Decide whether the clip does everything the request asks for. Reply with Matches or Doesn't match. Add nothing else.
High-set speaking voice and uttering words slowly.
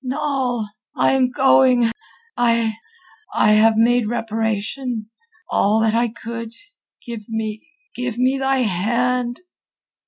Matches